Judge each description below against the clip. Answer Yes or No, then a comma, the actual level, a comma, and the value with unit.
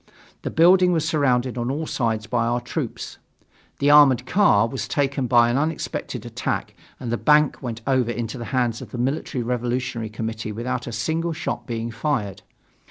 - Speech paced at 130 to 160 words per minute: No, average, 175 wpm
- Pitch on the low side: Yes, low, 125 Hz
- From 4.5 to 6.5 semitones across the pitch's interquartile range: No, average, 3.7 semitones